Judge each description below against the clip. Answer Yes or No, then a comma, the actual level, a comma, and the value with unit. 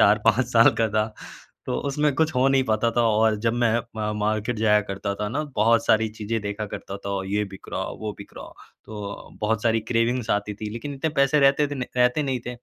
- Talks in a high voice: No, low, 110 Hz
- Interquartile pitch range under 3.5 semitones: Yes, average, 2.8 semitones